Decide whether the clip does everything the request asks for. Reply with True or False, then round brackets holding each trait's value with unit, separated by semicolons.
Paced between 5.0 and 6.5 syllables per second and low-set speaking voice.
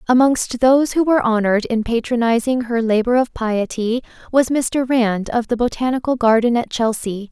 False (5.1 syllables/s; 240 Hz)